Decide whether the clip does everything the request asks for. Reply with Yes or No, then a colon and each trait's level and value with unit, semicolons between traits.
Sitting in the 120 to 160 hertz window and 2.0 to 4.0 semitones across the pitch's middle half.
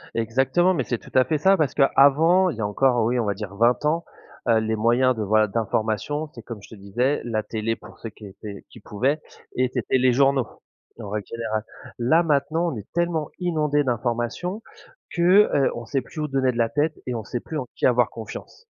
No: low, 125 Hz; average, 5.1 semitones